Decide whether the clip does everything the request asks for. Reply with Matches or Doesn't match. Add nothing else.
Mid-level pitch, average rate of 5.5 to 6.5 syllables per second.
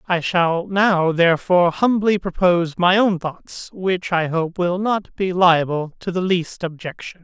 Doesn't match